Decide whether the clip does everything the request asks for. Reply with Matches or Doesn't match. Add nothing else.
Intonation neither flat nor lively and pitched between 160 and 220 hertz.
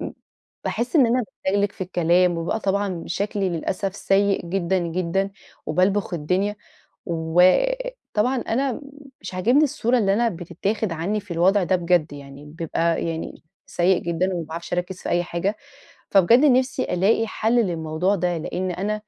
Matches